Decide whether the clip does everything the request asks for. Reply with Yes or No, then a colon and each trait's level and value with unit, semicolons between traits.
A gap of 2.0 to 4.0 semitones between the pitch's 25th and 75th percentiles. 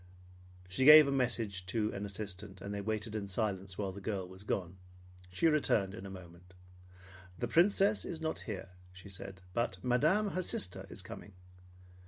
No: average, 4.7 semitones